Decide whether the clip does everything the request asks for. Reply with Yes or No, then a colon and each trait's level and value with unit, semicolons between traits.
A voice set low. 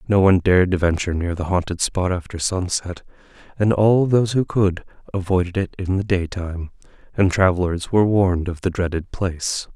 Yes: very low, 95 Hz